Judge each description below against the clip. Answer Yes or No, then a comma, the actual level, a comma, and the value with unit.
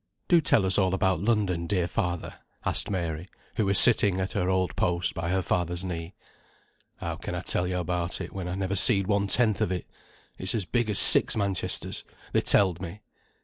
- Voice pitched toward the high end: No, very low, 95 Hz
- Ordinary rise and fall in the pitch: No, narrow, 2.2 semitones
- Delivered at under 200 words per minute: No, fast, 205 wpm